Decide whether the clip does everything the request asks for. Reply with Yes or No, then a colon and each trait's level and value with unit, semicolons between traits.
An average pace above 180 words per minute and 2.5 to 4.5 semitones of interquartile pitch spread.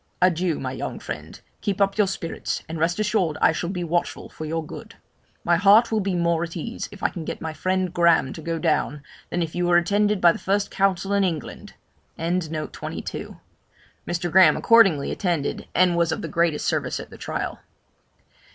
Yes: average, 190 wpm; average, 2.9 semitones